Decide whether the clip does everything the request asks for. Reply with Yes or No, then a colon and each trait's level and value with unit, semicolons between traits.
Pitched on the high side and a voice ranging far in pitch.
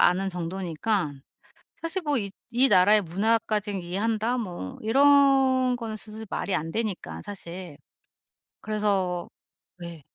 No: high, 210 Hz; average, 4.2 semitones